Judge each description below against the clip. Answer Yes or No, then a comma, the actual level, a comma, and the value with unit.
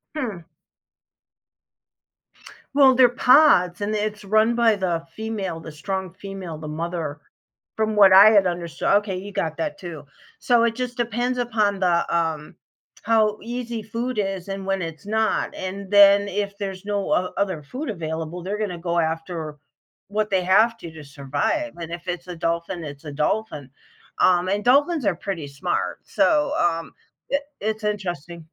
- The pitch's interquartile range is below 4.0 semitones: No, average, 4.3 semitones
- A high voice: Yes, high, 195 Hz